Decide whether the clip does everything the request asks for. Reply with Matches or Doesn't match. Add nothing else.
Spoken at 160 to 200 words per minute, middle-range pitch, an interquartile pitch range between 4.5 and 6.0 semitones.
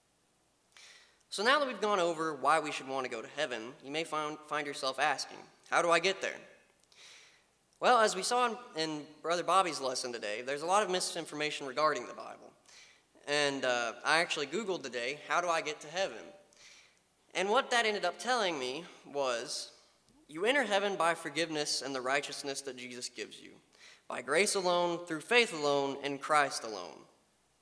Matches